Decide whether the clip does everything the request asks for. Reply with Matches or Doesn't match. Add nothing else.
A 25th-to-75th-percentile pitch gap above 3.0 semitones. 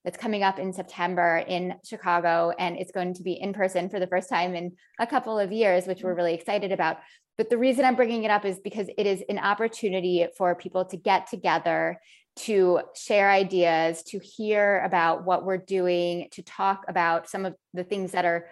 Doesn't match